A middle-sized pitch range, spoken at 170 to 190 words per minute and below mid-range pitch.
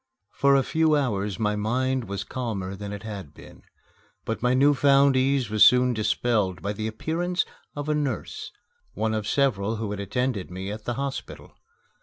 Yes: average, 4.9 semitones; average, 180 wpm; low, 115 Hz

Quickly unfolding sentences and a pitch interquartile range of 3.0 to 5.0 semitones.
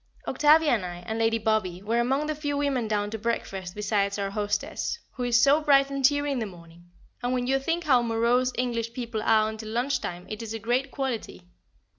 Yes: fast, 215 wpm; average, 4.2 semitones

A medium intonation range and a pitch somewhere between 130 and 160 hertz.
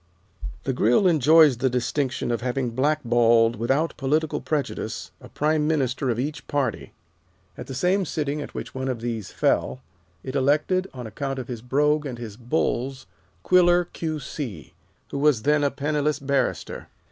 Yes: average, 3.7 semitones; low, 135 Hz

